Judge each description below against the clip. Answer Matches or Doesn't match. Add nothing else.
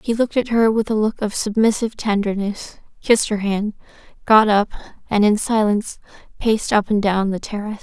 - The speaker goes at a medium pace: Matches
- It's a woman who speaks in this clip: Matches